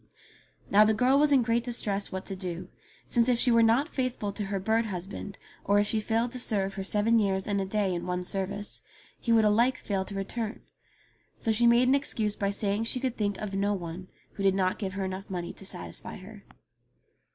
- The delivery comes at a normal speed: No, fast, 220 wpm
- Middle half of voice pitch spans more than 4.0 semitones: No, average, 3.0 semitones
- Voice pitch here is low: No, high, 205 Hz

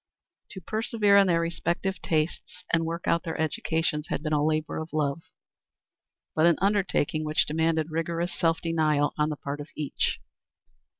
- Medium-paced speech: Yes, average, 165 wpm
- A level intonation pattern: Yes, narrow, 1.9 semitones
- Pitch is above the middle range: No, medium, 160 Hz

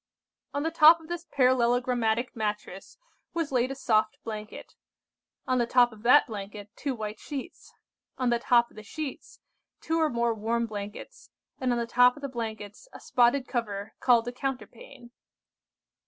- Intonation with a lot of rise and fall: No, average, 3.5 semitones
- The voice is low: No, high, 240 Hz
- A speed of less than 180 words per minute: Yes, average, 170 wpm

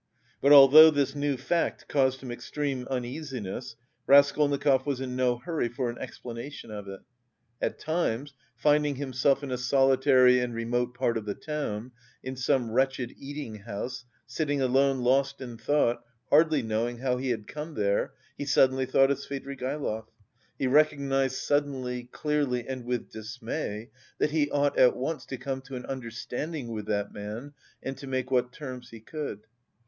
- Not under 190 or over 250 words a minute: No, average, 165 wpm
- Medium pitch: No, low, 130 Hz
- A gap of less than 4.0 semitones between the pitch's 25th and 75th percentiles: Yes, average, 2.8 semitones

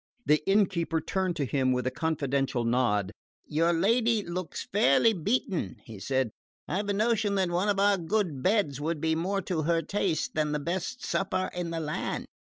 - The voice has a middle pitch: Yes, medium, 170 Hz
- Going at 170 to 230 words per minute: Yes, average, 180 wpm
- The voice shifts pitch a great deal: No, average, 5.0 semitones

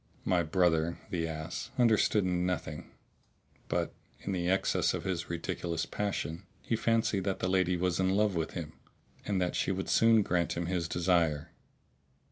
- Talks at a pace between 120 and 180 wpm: Yes, average, 160 wpm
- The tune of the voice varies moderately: No, narrow, 2.3 semitones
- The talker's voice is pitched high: No, very low, 90 Hz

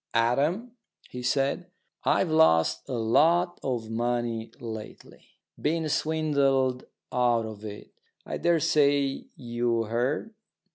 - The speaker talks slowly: Yes, slow, 105 wpm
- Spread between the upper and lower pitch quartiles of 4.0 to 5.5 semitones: Yes, average, 5.0 semitones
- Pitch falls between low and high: No, low, 125 Hz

